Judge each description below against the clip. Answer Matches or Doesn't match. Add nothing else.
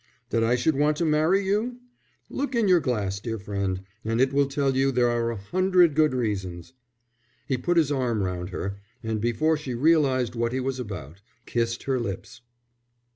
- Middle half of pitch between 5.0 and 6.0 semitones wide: Matches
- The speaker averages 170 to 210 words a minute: Matches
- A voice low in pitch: Matches